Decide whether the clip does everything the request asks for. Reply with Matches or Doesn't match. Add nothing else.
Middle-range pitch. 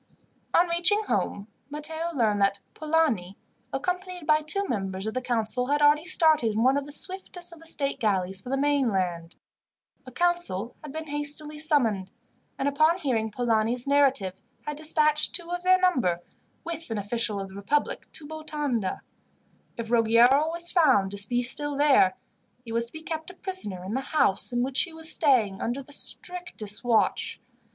Doesn't match